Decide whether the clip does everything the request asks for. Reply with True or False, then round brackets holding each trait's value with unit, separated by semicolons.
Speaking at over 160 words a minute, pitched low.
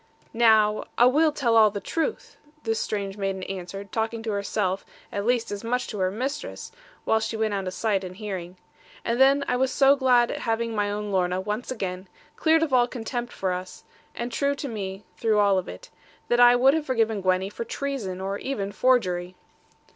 False (205 wpm; 220 Hz)